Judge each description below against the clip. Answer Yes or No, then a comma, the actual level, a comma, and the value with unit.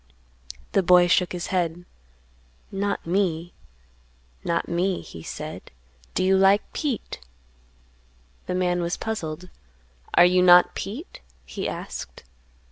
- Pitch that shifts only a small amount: Yes, narrow, 2.0 semitones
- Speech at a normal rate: No, slow, 120 wpm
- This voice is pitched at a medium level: Yes, medium, 180 Hz